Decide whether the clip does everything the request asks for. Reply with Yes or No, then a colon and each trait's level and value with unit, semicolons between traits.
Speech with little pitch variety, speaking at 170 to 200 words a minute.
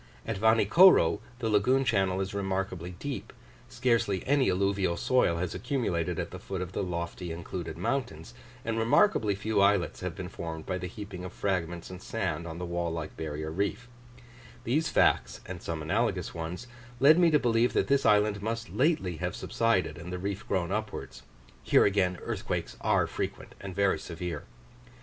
No: average, 4.4 semitones; average, 175 wpm